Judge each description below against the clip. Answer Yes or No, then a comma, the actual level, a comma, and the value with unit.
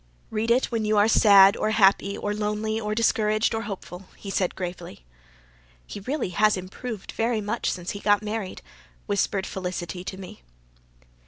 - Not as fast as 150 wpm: No, average, 165 wpm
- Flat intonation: Yes, narrow, 2.3 semitones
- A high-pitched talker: Yes, high, 205 Hz